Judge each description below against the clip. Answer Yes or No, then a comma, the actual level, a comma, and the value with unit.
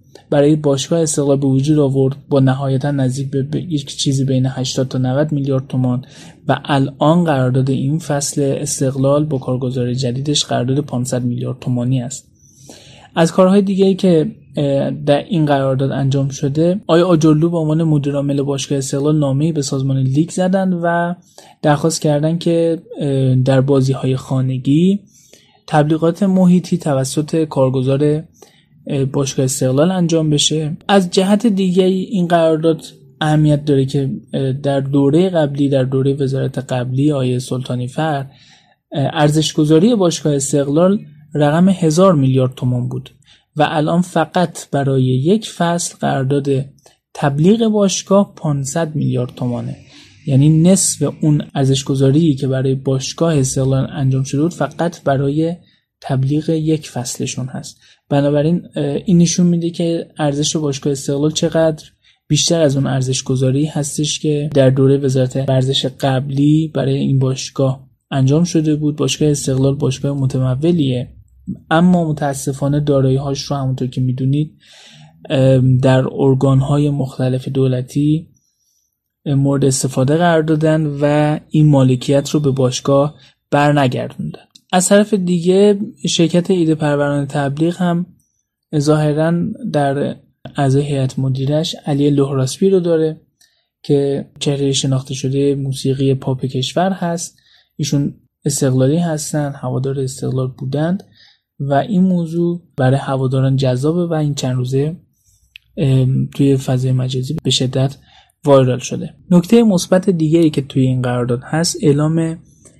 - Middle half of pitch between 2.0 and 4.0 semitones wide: Yes, average, 3.2 semitones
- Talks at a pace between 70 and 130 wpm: Yes, average, 125 wpm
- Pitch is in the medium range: Yes, medium, 145 Hz